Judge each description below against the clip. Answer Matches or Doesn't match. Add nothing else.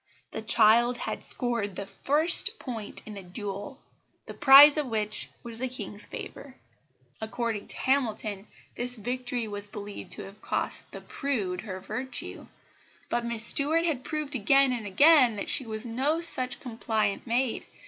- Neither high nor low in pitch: Doesn't match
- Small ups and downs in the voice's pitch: Doesn't match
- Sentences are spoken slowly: Doesn't match